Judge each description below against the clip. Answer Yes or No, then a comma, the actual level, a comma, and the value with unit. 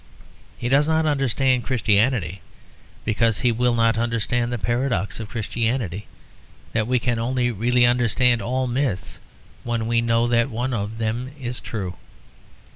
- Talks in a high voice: No, low, 120 Hz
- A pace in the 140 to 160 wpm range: Yes, average, 145 wpm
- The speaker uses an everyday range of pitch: No, narrow, 1.9 semitones